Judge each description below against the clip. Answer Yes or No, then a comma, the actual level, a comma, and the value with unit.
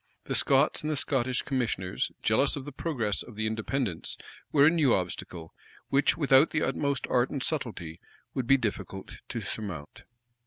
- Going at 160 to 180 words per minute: Yes, average, 170 wpm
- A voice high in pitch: No, low, 130 Hz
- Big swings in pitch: No, average, 5.0 semitones